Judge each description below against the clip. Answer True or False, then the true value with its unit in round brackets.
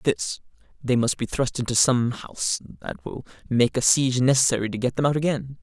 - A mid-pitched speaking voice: False (130 Hz)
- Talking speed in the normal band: True (190 wpm)